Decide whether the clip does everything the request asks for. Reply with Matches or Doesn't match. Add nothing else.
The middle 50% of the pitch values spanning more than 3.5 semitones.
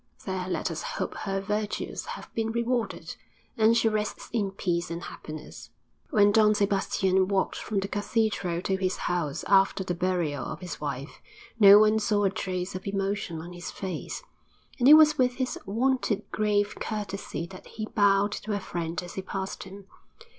Doesn't match